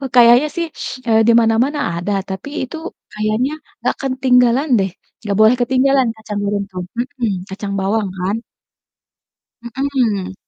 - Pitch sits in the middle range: No, high, 235 Hz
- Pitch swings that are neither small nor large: Yes, average, 4.0 semitones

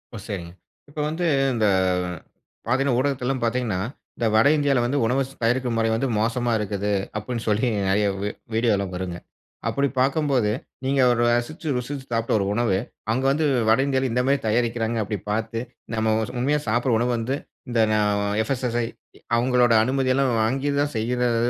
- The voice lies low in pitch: Yes, low, 120 Hz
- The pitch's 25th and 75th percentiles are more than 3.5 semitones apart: No, average, 3.0 semitones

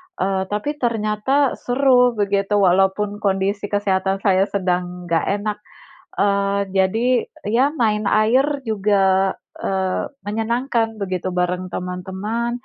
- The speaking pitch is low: No, high, 205 Hz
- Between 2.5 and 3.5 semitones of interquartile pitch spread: Yes, average, 2.9 semitones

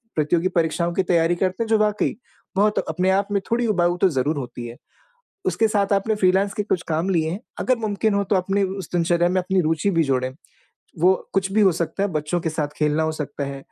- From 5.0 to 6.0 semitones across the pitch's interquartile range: No, average, 3.9 semitones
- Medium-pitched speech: Yes, medium, 180 Hz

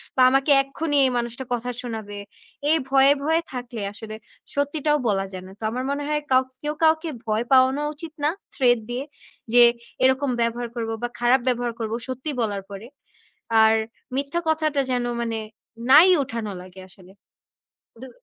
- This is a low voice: No, very high, 250 Hz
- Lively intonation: No, average, 3.9 semitones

